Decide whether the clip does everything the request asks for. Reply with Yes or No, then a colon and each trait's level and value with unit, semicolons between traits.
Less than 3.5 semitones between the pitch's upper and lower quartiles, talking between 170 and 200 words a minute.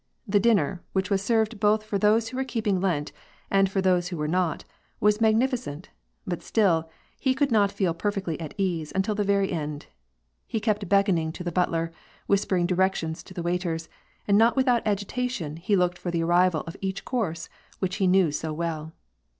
No: average, 3.8 semitones; average, 185 wpm